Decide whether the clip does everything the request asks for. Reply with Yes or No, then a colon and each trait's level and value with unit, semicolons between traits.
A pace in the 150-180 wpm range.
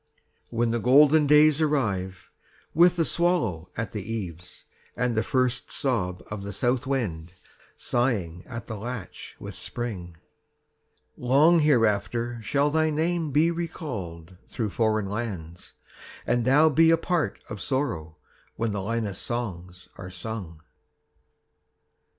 No: slow, 135 wpm